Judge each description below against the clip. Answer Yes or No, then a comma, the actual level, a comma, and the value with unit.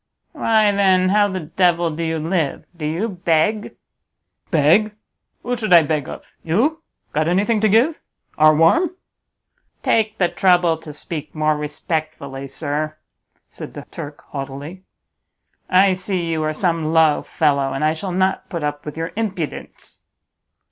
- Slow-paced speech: No, average, 150 wpm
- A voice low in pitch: No, medium, 165 Hz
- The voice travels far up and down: No, average, 4.1 semitones